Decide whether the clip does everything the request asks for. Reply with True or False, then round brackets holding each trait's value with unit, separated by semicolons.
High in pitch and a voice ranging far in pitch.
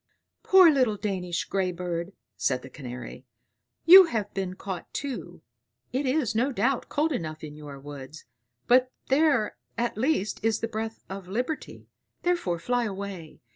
True (205 Hz; 6.8 semitones)